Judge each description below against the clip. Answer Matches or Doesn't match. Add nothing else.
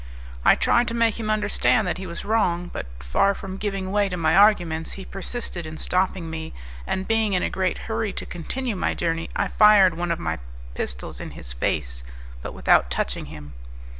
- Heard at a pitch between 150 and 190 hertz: Matches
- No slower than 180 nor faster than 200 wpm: Matches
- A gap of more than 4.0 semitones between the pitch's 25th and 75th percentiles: Matches